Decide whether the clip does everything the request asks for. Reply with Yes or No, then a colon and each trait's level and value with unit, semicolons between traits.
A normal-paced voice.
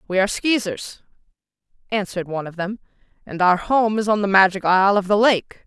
Yes: average, 190 wpm